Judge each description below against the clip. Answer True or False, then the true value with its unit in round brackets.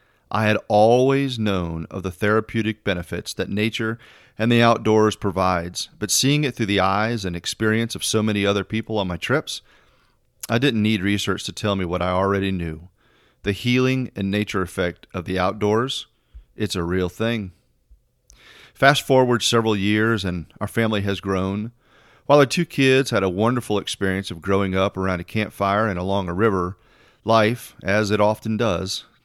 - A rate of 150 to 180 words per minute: True (175 wpm)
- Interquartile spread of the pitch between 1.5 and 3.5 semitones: True (3.0 semitones)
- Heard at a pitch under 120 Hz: True (105 Hz)